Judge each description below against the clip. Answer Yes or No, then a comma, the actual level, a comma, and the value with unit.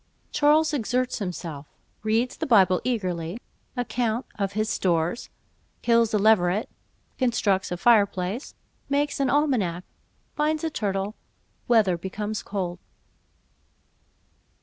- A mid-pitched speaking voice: No, high, 215 Hz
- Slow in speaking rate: Yes, slow, 80 wpm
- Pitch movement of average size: Yes, average, 4.9 semitones